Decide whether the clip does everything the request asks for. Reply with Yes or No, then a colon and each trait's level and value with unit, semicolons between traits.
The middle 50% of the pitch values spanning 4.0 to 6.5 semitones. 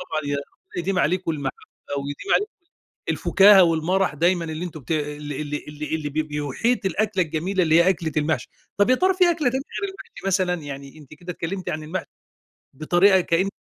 Yes: average, 4.3 semitones